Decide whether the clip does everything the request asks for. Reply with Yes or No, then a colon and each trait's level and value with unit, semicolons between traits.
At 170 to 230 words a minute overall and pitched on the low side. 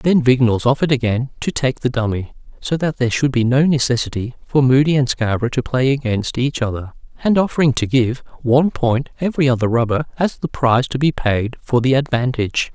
Yes: average, 200 wpm; low, 130 Hz